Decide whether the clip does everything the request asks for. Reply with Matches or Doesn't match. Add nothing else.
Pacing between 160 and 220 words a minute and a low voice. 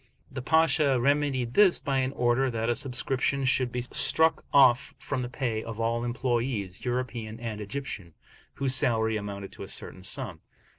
Matches